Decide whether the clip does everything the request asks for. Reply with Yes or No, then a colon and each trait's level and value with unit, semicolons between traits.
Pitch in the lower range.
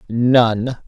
Yes: low, 120 Hz